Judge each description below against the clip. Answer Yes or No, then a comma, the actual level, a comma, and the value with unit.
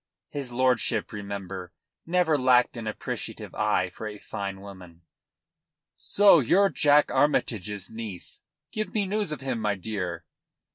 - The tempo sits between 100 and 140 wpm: Yes, slow, 135 wpm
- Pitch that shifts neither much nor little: No, wide, 6.7 semitones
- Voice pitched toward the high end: No, low, 115 Hz